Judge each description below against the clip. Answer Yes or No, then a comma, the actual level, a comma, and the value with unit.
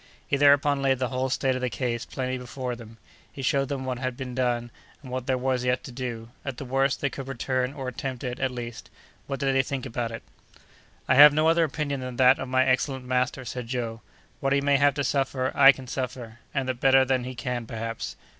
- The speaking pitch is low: Yes, low, 130 Hz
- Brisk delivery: Yes, fast, 230 wpm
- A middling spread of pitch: No, narrow, 1.5 semitones